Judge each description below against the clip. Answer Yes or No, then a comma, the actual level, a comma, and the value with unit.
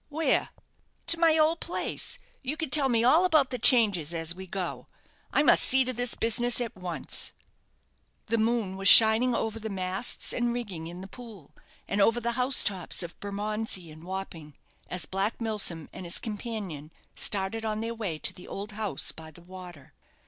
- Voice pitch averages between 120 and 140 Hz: No, high, 215 Hz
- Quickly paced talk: No, average, 185 wpm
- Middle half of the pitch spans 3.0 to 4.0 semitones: No, average, 4.7 semitones